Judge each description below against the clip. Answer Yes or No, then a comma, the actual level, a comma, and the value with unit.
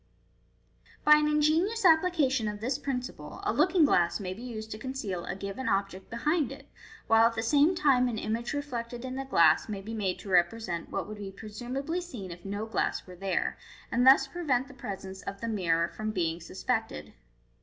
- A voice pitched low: No, high, 230 Hz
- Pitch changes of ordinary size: No, wide, 5.8 semitones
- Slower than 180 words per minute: No, average, 190 wpm